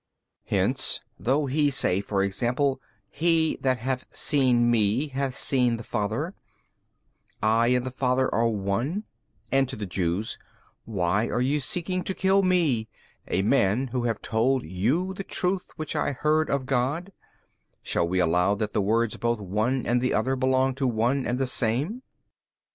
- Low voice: Yes, low, 125 Hz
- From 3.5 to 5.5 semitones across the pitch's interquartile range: Yes, average, 4.2 semitones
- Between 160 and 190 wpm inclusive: Yes, average, 165 wpm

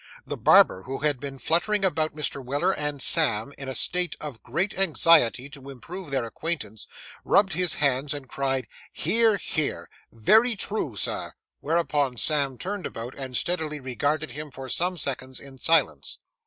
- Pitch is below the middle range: No, medium, 145 Hz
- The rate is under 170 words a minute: Yes, average, 160 wpm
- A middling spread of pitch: Yes, average, 4.3 semitones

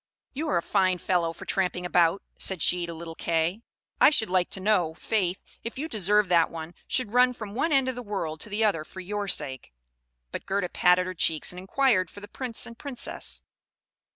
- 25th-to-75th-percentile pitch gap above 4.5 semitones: No, average, 4.2 semitones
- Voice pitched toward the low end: No, high, 190 Hz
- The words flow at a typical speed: No, fast, 210 wpm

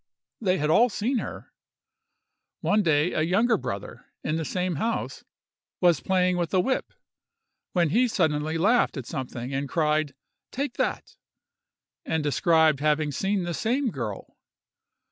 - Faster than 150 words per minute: No, average, 145 wpm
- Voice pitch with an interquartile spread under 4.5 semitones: No, average, 5.2 semitones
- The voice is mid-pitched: Yes, medium, 170 Hz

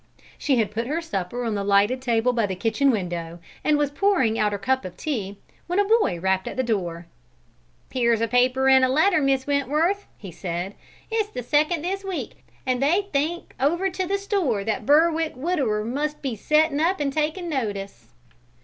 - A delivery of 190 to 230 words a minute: Yes, average, 195 wpm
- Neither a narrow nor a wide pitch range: No, wide, 6.8 semitones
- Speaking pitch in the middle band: No, very high, 265 Hz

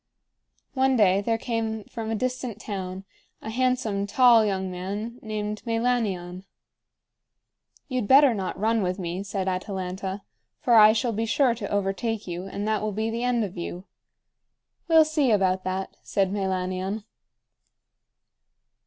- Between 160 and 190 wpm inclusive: No, average, 145 wpm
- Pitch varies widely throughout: No, average, 3.3 semitones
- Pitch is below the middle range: No, high, 210 Hz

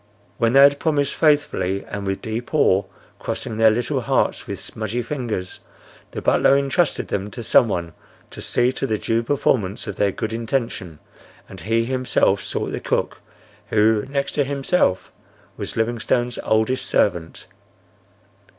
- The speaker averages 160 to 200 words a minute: No, average, 150 wpm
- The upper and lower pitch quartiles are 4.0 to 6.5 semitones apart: Yes, average, 4.5 semitones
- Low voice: Yes, low, 115 Hz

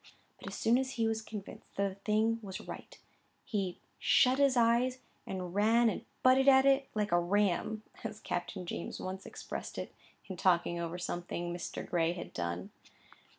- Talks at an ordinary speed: Yes, average, 175 wpm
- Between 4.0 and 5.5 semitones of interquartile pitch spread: Yes, average, 4.8 semitones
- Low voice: No, high, 205 Hz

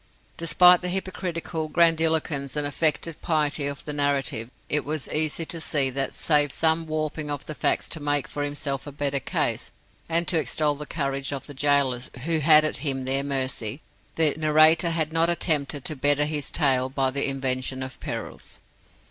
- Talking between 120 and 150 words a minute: No, average, 175 wpm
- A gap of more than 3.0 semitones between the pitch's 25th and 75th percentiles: No, narrow, 2.5 semitones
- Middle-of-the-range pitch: Yes, medium, 145 Hz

